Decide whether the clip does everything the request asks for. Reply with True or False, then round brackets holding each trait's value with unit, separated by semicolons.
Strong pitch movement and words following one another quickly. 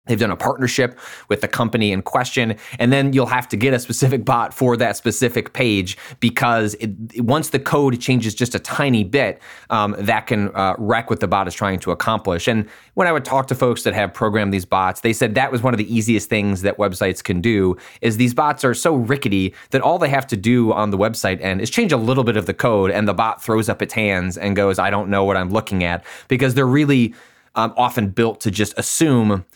False (3.7 semitones; 240 wpm)